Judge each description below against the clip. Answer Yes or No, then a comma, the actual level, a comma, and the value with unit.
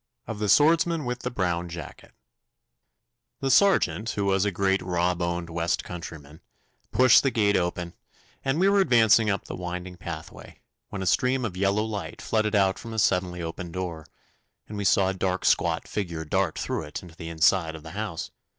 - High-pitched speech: No, very low, 95 Hz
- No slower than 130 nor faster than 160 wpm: No, average, 185 wpm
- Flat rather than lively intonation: No, average, 4.0 semitones